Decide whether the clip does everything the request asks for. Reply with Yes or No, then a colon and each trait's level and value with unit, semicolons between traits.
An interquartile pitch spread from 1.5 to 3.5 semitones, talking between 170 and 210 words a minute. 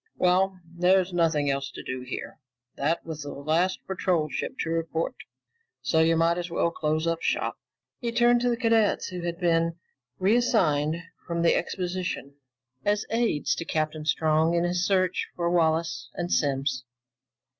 No: average, 2.8 semitones; average, 160 wpm